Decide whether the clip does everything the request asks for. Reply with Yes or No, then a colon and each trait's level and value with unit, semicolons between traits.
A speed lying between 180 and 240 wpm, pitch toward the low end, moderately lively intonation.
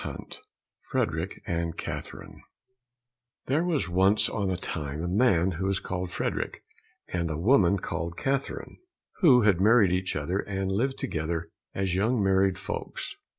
No: average, 150 wpm; very low, 95 Hz; average, 3.6 semitones